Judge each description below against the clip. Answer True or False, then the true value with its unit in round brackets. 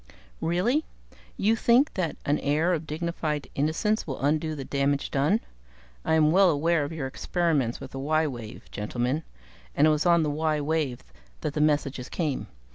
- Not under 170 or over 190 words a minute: True (175 wpm)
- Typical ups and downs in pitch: True (3.1 semitones)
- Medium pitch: True (155 Hz)